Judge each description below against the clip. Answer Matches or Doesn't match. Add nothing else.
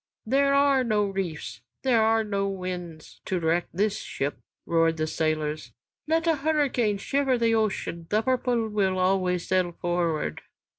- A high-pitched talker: Matches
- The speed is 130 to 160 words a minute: Matches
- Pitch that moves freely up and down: Matches